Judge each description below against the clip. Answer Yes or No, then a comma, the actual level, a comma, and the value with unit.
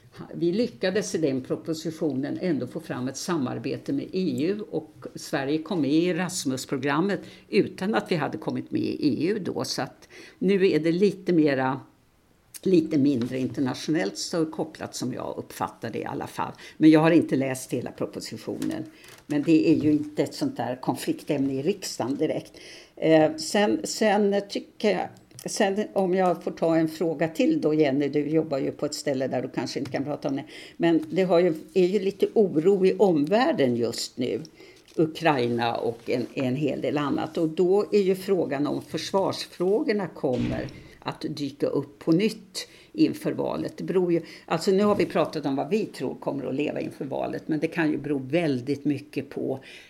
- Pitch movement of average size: Yes, average, 4.6 semitones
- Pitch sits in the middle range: Yes, medium, 160 Hz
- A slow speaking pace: No, average, 185 wpm